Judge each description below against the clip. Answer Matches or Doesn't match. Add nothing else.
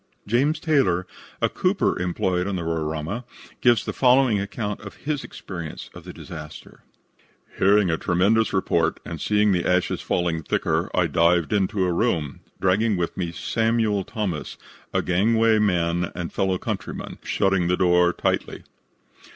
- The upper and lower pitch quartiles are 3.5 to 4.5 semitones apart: Matches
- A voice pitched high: Doesn't match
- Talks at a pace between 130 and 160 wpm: Matches